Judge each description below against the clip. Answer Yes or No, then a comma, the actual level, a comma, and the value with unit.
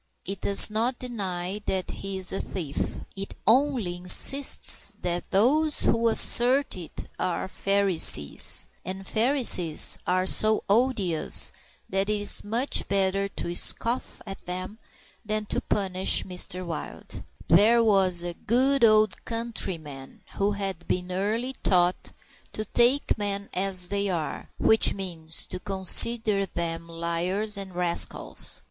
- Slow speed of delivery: Yes, slow, 130 wpm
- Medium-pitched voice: No, high, 195 Hz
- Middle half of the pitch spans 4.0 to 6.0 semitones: No, average, 3.5 semitones